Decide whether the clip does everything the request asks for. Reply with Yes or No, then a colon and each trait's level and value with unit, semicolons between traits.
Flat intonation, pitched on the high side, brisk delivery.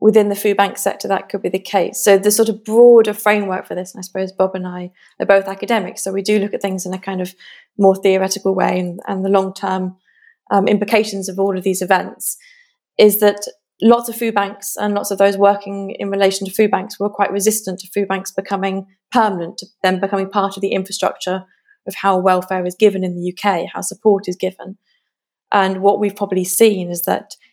Yes: narrow, 1.7 semitones; high, 195 Hz; fast, 220 wpm